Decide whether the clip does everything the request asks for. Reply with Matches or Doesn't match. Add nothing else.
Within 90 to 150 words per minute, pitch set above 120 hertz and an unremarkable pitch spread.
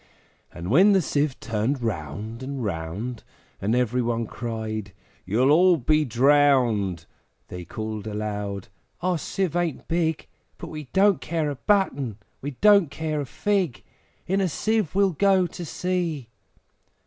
Doesn't match